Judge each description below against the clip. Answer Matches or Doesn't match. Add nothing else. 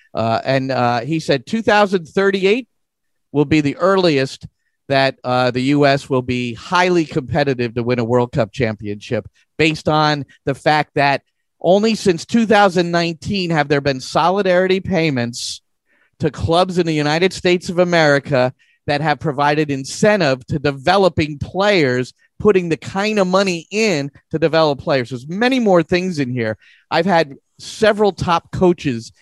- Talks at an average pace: Matches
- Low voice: Doesn't match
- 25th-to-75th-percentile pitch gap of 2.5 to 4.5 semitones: Doesn't match